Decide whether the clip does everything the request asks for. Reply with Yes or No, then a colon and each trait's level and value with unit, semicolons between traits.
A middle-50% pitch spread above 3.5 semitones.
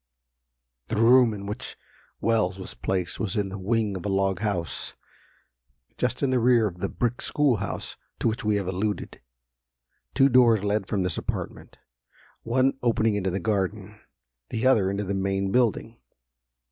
No: average, 3.0 semitones